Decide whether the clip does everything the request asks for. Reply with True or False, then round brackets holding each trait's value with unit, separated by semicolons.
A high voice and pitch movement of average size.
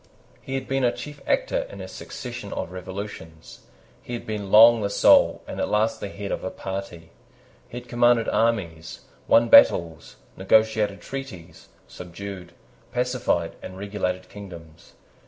False (100 Hz; 4.6 semitones)